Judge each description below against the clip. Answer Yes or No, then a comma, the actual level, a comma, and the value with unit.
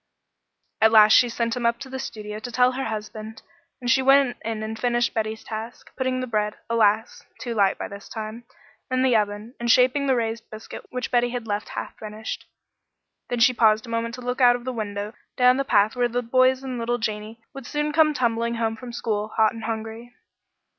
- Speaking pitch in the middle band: No, high, 230 Hz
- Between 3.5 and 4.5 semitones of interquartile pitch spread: No, narrow, 2.4 semitones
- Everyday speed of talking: No, fast, 215 wpm